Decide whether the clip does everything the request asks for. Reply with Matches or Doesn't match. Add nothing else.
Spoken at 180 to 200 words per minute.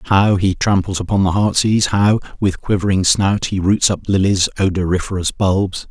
Doesn't match